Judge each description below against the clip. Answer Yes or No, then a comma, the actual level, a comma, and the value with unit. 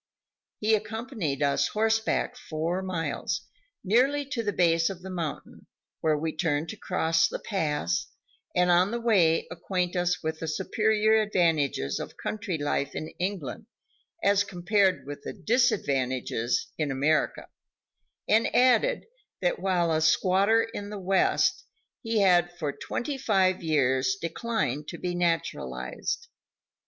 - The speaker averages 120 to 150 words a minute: Yes, slow, 135 wpm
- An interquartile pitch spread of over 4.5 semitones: Yes, average, 5.2 semitones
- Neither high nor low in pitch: Yes, medium, 180 Hz